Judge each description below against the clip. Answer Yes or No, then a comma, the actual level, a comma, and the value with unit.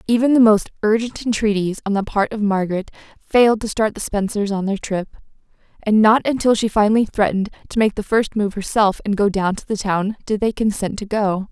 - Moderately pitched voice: No, high, 210 Hz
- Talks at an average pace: No, fast, 215 wpm